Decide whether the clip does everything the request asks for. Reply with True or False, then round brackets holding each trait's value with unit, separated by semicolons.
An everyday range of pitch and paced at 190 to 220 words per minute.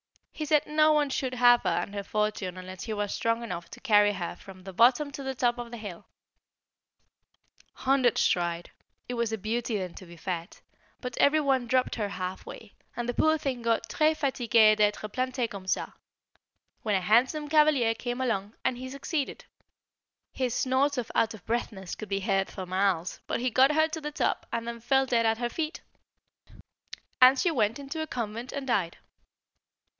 True (4.5 semitones; 195 wpm)